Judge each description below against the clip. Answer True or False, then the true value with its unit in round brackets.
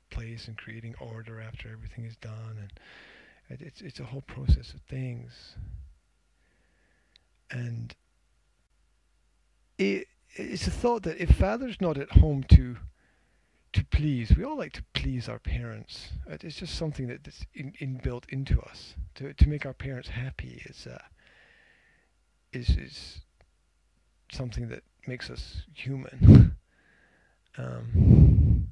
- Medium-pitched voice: False (110 Hz)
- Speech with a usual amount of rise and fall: False (7.9 semitones)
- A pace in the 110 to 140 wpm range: True (135 wpm)